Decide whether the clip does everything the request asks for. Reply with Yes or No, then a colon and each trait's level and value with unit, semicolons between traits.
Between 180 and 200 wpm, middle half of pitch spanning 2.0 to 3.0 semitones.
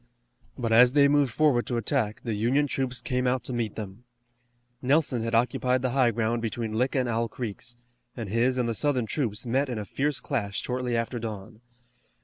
Yes: average, 195 wpm; narrow, 2.4 semitones